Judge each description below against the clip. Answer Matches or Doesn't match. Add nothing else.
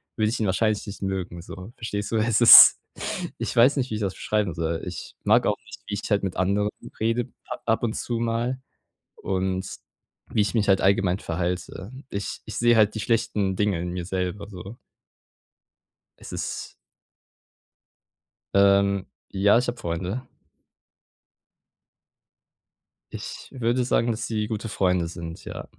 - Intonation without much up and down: Doesn't match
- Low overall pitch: Matches